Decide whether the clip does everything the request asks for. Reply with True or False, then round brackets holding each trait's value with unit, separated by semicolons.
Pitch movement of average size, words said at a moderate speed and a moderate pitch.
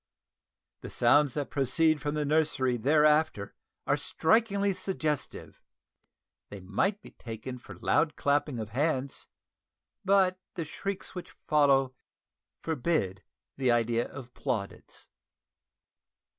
False (4.7 semitones; 110 wpm; 145 Hz)